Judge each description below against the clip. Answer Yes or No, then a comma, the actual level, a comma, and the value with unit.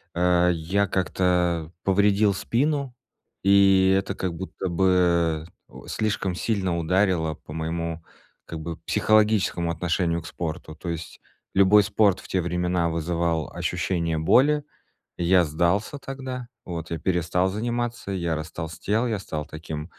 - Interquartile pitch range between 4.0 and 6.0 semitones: No, average, 3.1 semitones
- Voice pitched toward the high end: No, very low, 90 Hz